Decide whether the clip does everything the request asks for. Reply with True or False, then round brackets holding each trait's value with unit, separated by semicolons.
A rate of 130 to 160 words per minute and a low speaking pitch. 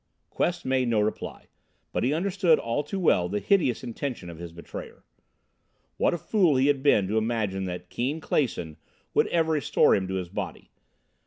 False (180 wpm; 125 Hz)